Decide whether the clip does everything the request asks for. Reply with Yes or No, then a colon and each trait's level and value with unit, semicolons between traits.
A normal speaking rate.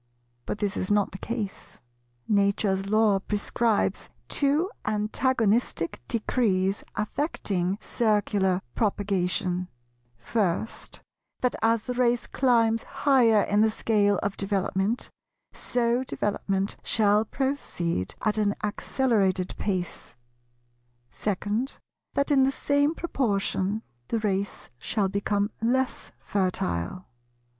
No: slow, 100 wpm